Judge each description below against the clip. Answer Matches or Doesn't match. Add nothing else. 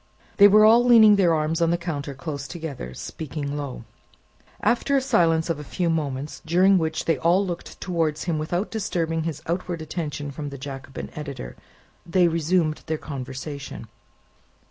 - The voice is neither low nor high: Matches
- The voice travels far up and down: Doesn't match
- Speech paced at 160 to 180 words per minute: Matches